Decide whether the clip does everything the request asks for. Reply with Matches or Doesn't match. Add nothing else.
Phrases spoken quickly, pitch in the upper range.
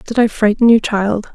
Matches